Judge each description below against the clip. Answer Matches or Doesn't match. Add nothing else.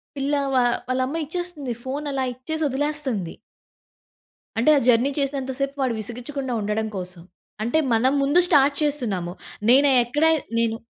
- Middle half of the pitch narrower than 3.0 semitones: Doesn't match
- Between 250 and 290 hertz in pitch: Matches